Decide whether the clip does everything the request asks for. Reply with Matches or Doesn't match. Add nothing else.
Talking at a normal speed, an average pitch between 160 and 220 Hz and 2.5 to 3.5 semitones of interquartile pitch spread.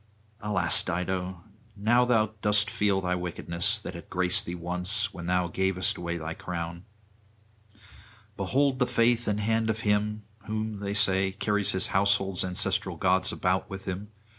Doesn't match